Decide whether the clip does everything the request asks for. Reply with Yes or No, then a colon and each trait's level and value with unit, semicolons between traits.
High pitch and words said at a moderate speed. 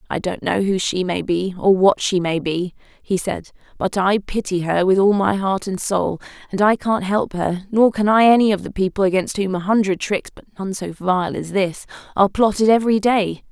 No: high, 195 Hz; fast, 225 wpm